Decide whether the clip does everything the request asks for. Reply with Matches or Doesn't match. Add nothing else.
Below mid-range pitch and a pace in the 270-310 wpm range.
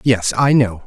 Doesn't match